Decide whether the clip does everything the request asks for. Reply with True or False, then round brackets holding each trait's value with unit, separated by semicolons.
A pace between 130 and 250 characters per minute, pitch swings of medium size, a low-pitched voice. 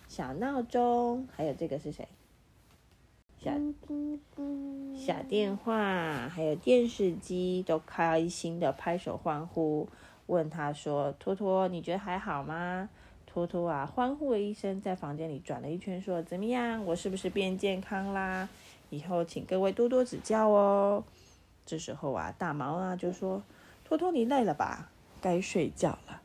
False (215 characters per minute; 4.7 semitones; 185 Hz)